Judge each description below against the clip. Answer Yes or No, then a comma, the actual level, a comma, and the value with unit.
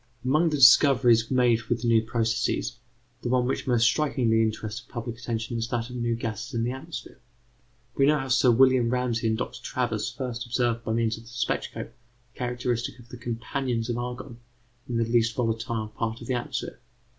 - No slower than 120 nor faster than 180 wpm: No, average, 190 wpm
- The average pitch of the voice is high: No, low, 120 Hz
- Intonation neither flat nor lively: No, narrow, 1.7 semitones